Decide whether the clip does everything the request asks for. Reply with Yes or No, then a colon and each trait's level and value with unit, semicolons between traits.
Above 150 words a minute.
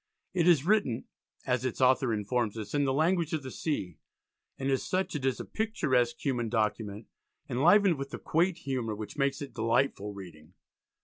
Yes: average, 180 wpm